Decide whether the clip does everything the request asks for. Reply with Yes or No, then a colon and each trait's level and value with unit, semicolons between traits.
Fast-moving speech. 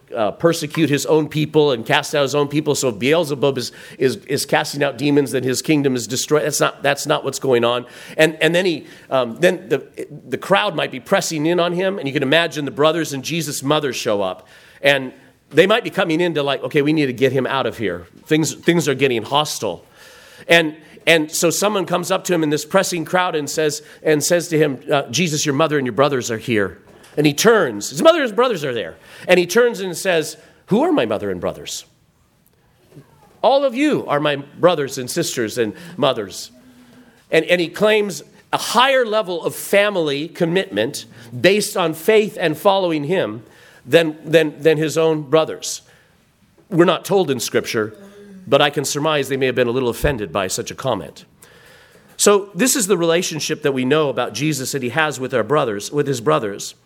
Yes: fast, 210 wpm